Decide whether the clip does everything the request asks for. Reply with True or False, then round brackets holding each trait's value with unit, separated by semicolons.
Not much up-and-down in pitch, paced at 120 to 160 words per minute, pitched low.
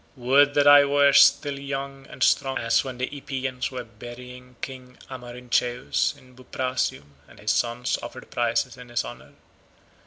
True (2.0 semitones; 155 wpm; 125 Hz)